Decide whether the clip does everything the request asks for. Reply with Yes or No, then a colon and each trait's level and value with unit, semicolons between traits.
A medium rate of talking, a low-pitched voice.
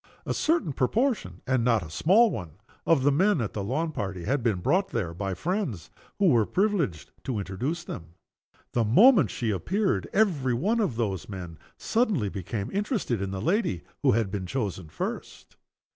Yes: average, 175 wpm; low, 125 Hz